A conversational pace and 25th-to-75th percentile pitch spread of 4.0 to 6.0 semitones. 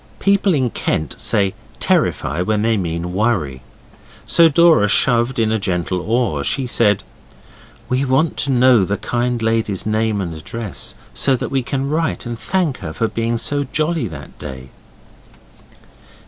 Yes: average, 155 wpm; wide, 5.5 semitones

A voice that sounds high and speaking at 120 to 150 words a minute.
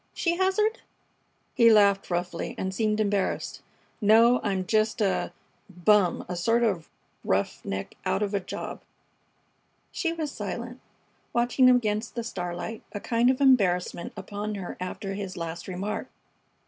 Yes: high, 210 Hz; average, 140 wpm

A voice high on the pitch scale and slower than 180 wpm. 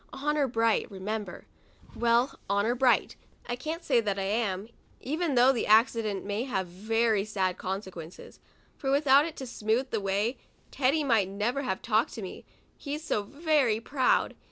Yes: high, 230 Hz; average, 160 wpm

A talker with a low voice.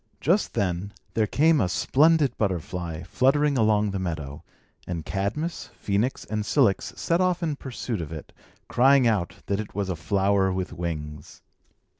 Yes: low, 100 Hz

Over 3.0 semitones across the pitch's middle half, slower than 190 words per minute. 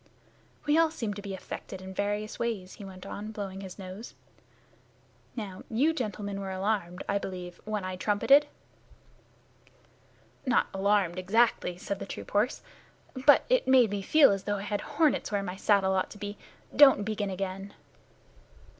No: average, 2.7 semitones; average, 165 wpm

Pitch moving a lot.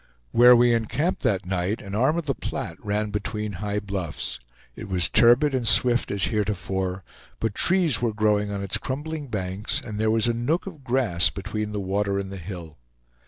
No: average, 3.7 semitones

